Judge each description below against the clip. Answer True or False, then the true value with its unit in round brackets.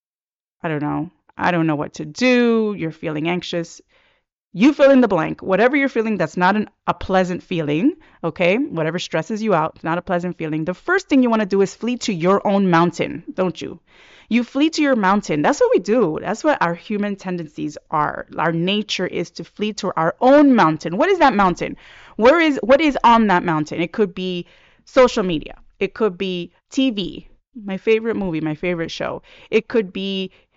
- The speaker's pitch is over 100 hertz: True (190 Hz)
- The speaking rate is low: False (205 wpm)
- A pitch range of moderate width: False (5.7 semitones)